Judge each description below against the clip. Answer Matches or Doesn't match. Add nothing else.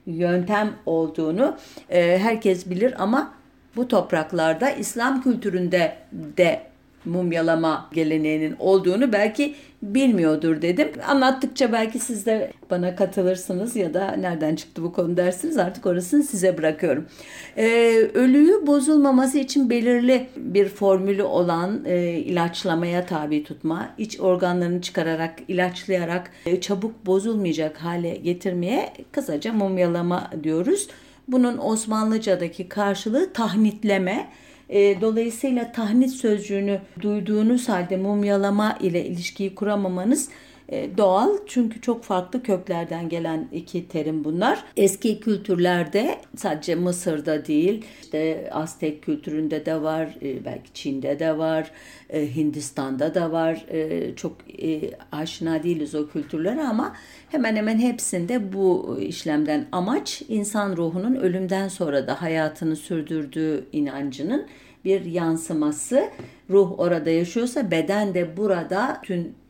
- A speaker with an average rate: Doesn't match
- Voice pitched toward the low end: Doesn't match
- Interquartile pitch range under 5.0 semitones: Doesn't match